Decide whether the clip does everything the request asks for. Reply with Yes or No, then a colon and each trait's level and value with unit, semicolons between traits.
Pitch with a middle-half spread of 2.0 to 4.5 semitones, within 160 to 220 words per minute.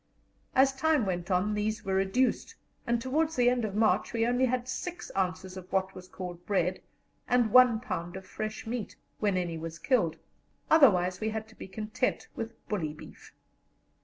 No: average, 5.0 semitones; average, 180 wpm